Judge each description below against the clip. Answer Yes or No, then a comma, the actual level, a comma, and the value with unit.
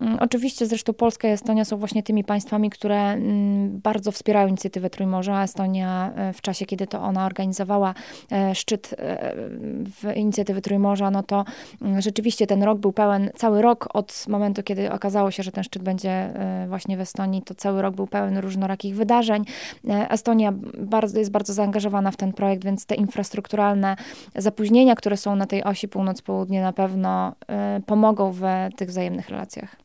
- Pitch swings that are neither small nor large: No, narrow, 1.7 semitones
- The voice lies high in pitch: Yes, high, 200 Hz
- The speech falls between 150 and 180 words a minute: Yes, average, 155 wpm